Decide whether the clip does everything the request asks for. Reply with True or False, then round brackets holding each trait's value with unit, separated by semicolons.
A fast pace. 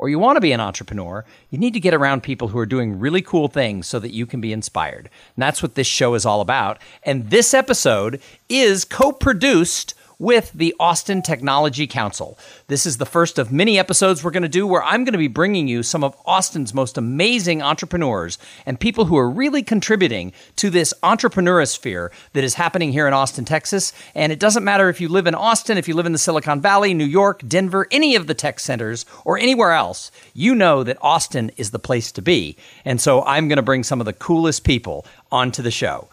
True (220 wpm)